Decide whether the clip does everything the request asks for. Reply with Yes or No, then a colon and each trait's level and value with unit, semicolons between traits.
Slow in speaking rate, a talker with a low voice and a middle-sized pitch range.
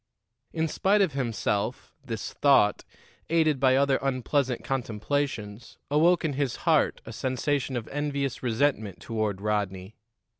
Yes: slow, 125 wpm; low, 130 Hz; average, 4.7 semitones